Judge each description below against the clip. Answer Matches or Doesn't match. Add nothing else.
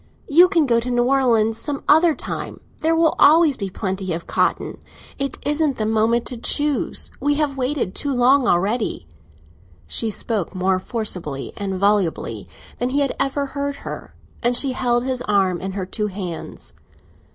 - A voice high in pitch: Matches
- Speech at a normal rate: Matches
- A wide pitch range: Matches